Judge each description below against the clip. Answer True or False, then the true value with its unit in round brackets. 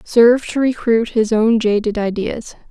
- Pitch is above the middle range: True (225 Hz)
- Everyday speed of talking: True (155 wpm)